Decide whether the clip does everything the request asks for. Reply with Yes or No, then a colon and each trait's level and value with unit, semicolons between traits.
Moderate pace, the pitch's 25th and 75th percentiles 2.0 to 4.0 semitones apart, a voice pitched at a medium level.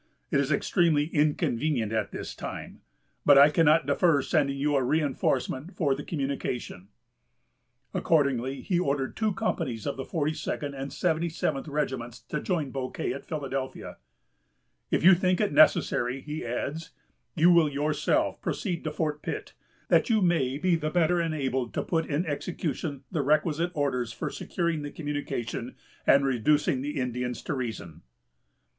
Yes: average, 150 wpm; average, 3.4 semitones; medium, 145 Hz